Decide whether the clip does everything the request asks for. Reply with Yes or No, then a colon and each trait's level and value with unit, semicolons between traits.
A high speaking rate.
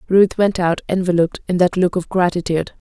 No: average, 185 wpm